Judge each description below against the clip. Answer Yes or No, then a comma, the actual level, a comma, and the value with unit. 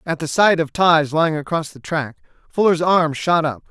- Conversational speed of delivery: No, fast, 210 wpm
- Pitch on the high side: No, medium, 160 Hz